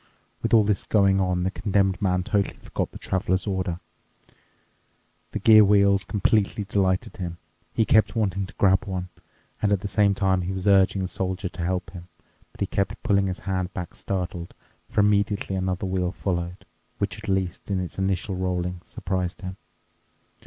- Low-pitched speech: Yes, very low, 95 Hz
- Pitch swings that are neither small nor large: No, narrow, 1.6 semitones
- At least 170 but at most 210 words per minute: Yes, average, 175 wpm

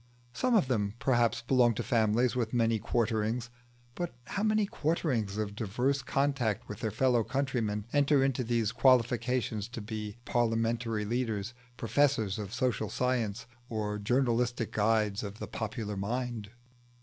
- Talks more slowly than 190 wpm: Yes, average, 140 wpm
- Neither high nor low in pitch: No, low, 115 Hz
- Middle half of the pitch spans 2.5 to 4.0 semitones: Yes, average, 2.9 semitones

